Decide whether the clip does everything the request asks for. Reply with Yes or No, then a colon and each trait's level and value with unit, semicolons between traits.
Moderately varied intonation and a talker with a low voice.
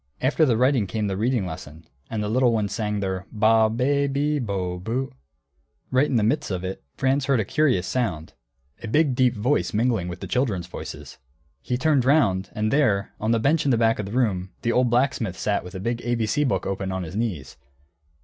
Yes: average, 5.0 semitones; low, 115 Hz